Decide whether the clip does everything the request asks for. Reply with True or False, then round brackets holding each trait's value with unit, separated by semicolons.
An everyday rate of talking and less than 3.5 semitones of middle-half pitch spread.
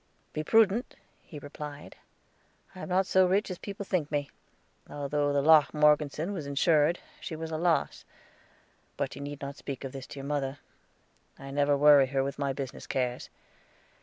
True (175 wpm; 2.7 semitones)